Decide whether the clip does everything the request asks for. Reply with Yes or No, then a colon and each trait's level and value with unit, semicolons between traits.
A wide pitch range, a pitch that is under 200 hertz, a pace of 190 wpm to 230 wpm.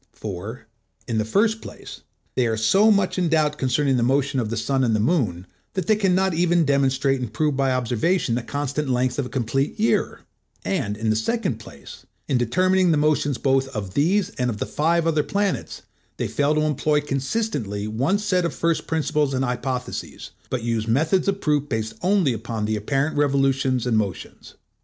Yes: wide, 5.8 semitones; low, 135 Hz; average, 195 wpm